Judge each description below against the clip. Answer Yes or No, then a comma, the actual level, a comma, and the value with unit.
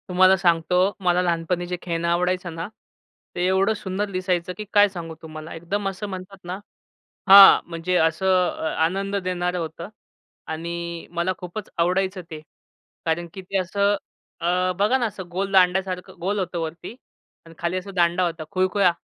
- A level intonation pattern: Yes, narrow, 2.0 semitones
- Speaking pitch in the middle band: Yes, medium, 180 Hz